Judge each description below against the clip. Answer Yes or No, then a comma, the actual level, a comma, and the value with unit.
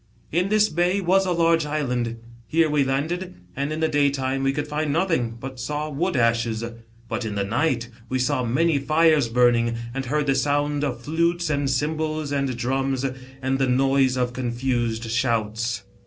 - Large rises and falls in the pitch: No, average, 4.0 semitones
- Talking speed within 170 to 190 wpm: Yes, average, 180 wpm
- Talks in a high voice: No, low, 135 Hz